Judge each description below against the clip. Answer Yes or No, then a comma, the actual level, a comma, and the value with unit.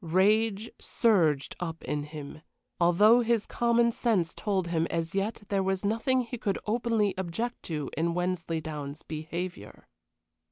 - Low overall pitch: No, high, 190 Hz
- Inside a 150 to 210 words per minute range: No, slow, 135 wpm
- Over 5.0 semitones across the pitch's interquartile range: Yes, wide, 5.4 semitones